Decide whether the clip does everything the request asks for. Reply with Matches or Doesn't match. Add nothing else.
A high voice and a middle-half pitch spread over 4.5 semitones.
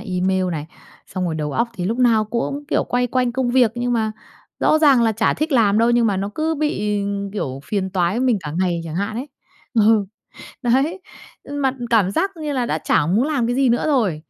Matches